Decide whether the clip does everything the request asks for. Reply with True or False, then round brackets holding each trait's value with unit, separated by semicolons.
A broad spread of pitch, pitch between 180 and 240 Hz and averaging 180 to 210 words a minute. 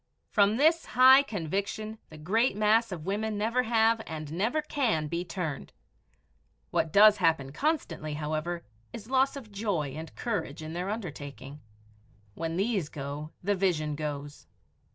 False (6.3 semitones; 190 Hz; 145 wpm)